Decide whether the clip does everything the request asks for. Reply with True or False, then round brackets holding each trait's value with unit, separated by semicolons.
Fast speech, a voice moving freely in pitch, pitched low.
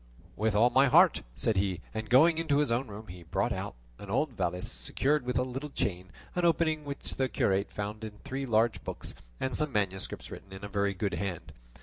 True (220 wpm; 5.7 semitones; 110 Hz)